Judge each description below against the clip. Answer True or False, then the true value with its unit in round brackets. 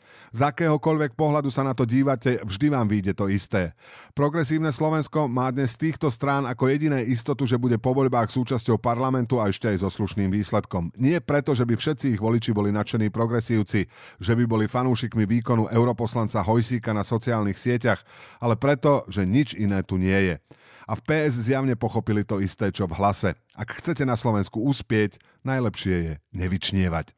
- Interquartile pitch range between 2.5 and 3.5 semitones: False (4.7 semitones)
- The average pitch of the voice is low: True (120 Hz)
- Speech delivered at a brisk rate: True (175 wpm)